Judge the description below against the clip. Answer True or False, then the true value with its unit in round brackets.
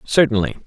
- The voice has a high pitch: False (125 Hz)